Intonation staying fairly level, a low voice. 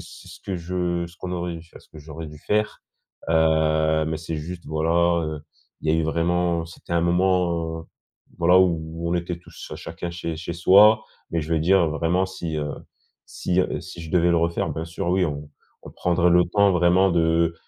Yes: narrow, 1.6 semitones; very low, 85 Hz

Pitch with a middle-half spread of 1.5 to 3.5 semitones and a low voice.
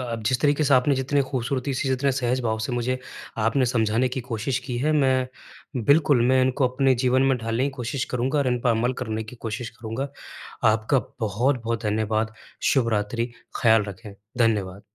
Yes: average, 2.8 semitones; low, 125 Hz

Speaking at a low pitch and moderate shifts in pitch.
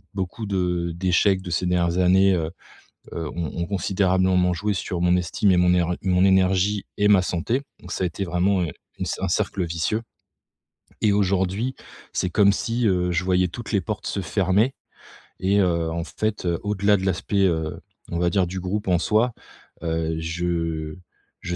No: very low, 90 Hz; narrow, 2.3 semitones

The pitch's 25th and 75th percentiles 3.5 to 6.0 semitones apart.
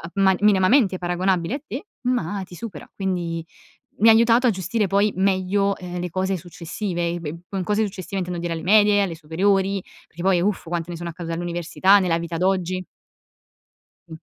No: narrow, 2.5 semitones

